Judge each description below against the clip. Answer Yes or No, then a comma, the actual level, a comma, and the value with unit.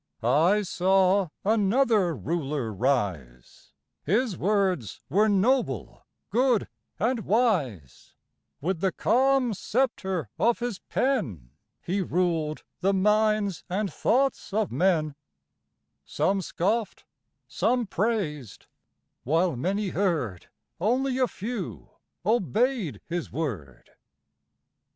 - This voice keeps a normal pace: No, slow, 95 wpm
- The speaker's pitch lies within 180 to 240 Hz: Yes, high, 190 Hz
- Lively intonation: Yes, wide, 6.2 semitones